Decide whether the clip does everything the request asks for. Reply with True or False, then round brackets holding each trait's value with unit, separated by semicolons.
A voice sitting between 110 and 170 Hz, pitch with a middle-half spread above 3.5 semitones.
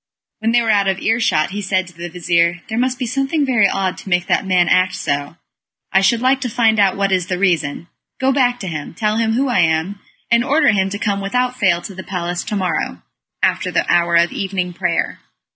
False (195 Hz; 4.6 semitones)